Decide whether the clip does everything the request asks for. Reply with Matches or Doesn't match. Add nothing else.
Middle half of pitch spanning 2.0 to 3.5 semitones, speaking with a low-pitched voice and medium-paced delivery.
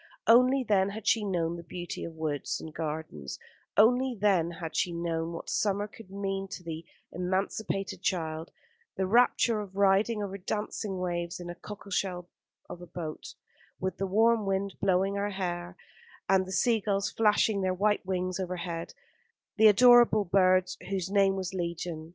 Doesn't match